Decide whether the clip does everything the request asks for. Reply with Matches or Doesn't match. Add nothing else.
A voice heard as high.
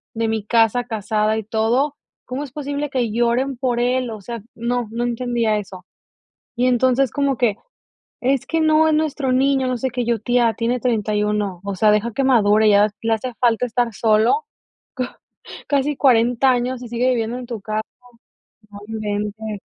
Matches